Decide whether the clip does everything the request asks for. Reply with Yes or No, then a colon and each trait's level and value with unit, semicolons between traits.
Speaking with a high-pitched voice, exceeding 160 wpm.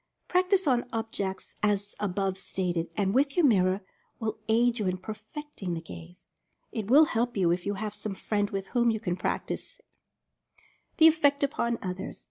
Yes: high, 210 Hz; average, 175 wpm